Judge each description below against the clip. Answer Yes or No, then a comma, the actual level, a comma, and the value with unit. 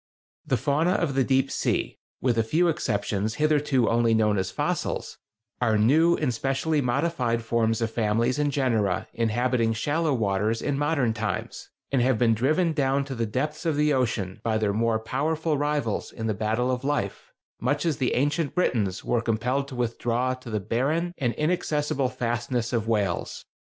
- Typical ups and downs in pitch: Yes, average, 4.4 semitones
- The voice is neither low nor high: No, low, 125 Hz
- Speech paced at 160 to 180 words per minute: Yes, average, 170 wpm